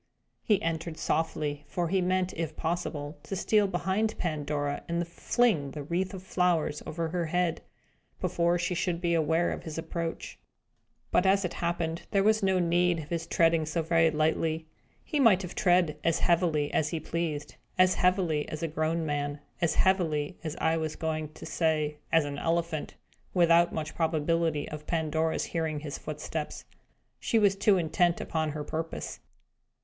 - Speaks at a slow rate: No, average, 165 wpm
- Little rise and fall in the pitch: Yes, narrow, 2.3 semitones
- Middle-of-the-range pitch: Yes, medium, 165 Hz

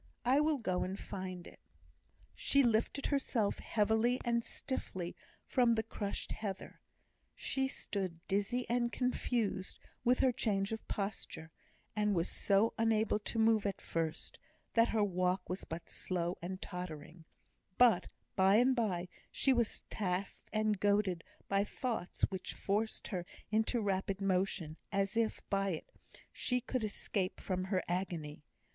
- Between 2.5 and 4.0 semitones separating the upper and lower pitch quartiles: Yes, average, 3.7 semitones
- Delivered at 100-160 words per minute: Yes, average, 145 wpm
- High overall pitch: Yes, high, 205 Hz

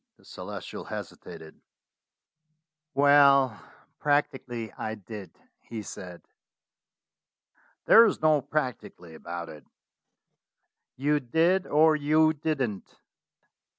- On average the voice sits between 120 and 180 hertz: Yes, medium, 140 Hz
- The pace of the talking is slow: Yes, slow, 85 wpm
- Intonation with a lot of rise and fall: Yes, wide, 6.2 semitones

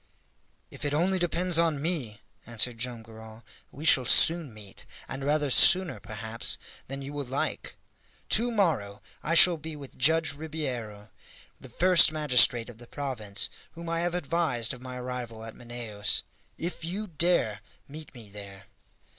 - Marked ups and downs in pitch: Yes, wide, 6.2 semitones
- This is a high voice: No, low, 135 Hz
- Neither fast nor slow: Yes, average, 155 wpm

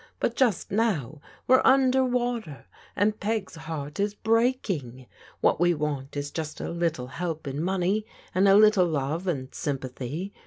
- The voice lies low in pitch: No, medium, 175 Hz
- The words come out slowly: No, average, 155 wpm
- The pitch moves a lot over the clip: Yes, wide, 6.7 semitones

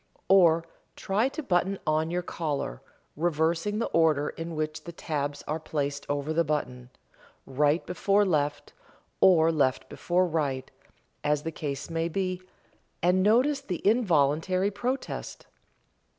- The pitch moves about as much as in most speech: Yes, average, 3.9 semitones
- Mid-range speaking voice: Yes, medium, 165 Hz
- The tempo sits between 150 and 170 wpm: No, slow, 135 wpm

